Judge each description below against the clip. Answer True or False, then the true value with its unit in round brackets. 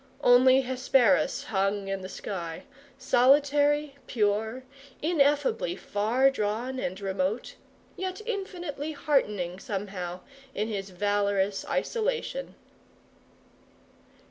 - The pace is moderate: False (90 wpm)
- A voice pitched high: True (245 Hz)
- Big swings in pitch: True (6.3 semitones)